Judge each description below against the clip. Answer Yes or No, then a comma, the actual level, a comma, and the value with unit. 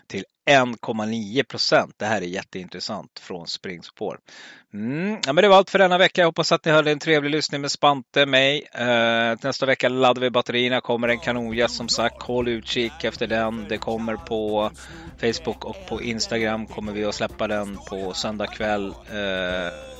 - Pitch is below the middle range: Yes, low, 115 Hz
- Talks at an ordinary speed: Yes, average, 175 wpm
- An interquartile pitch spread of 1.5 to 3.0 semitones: No, average, 3.9 semitones